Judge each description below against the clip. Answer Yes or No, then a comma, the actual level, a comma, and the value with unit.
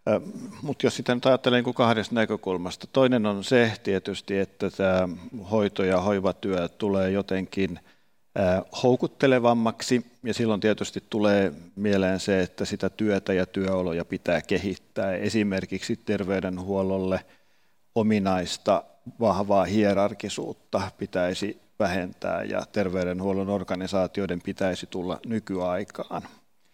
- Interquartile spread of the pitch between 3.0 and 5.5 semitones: No, narrow, 2.6 semitones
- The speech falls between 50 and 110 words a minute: Yes, average, 105 wpm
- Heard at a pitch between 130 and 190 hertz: No, low, 100 Hz